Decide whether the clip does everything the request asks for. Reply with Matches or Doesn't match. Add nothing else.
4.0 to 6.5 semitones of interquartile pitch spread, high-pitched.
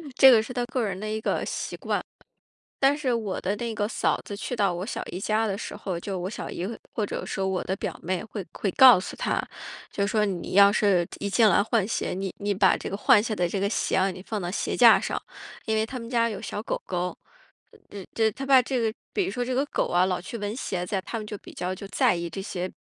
Doesn't match